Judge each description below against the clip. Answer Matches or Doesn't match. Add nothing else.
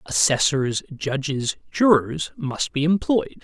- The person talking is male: Matches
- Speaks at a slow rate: Matches